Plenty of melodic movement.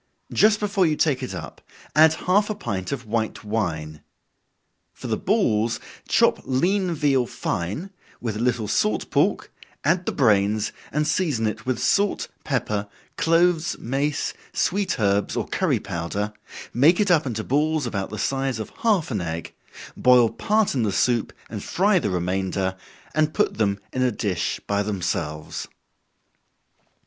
Yes: wide, 7.4 semitones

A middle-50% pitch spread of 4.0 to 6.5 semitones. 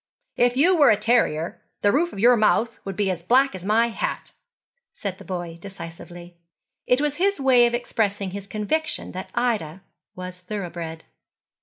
Yes: average, 5.2 semitones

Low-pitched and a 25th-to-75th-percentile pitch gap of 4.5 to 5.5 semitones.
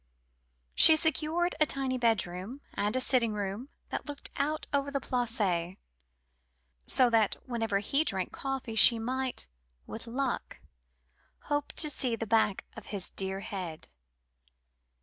No: high, 235 Hz; average, 5.1 semitones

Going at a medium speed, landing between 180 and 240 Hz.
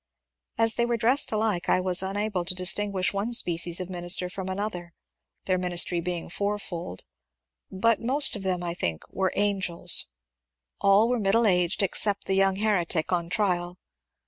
Yes: average, 170 wpm; high, 190 Hz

